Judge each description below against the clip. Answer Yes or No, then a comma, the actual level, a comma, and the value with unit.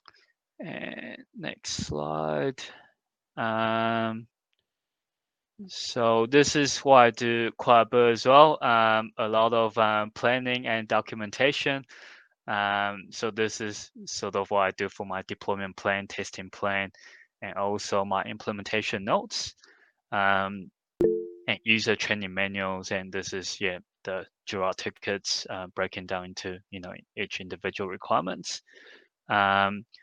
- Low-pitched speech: Yes, low, 105 Hz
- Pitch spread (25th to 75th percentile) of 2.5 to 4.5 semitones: Yes, average, 3.0 semitones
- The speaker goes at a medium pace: No, slow, 130 wpm